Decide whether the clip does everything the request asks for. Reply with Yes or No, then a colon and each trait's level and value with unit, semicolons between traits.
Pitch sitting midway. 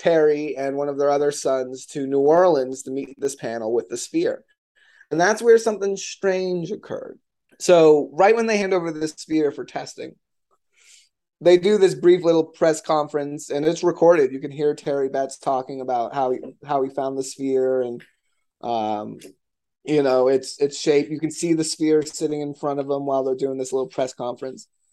Yes: medium, 150 Hz